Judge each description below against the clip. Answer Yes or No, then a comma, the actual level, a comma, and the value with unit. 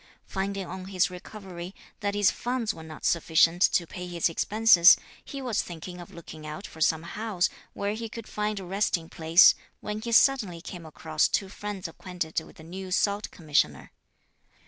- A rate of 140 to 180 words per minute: Yes, average, 175 wpm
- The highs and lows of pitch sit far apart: No, average, 3.6 semitones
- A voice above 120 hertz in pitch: Yes, medium, 185 Hz